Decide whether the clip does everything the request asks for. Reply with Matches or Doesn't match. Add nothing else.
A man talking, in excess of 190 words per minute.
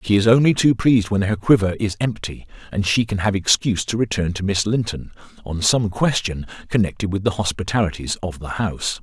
Matches